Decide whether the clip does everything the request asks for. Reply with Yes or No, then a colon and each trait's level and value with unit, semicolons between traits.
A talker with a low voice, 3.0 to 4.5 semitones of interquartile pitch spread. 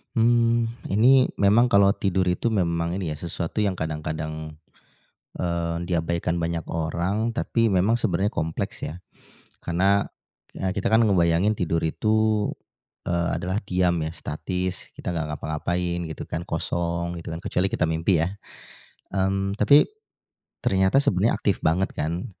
Yes: very low, 90 Hz; average, 3.4 semitones